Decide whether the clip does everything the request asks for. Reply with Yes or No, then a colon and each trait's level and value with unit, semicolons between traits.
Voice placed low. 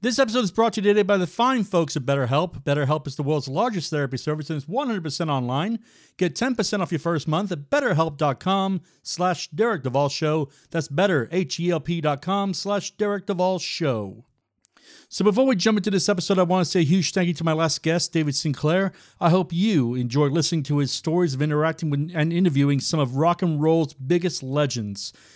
No: medium, 165 Hz